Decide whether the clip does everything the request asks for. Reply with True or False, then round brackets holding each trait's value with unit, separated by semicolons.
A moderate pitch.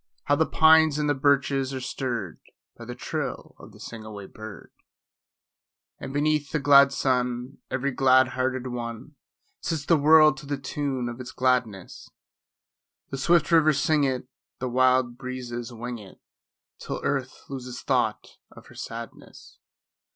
False (130 Hz)